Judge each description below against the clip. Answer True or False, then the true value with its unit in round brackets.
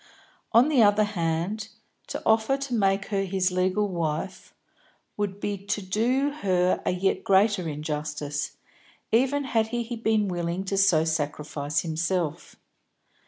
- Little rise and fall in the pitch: False (4.5 semitones)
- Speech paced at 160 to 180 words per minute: False (135 wpm)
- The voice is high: True (195 Hz)